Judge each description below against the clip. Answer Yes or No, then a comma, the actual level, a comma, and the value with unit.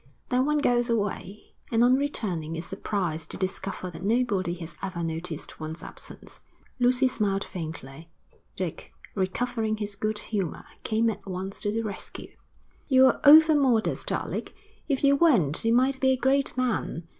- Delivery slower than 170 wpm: Yes, average, 155 wpm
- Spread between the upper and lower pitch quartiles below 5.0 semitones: No, wide, 5.6 semitones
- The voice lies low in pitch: No, high, 215 Hz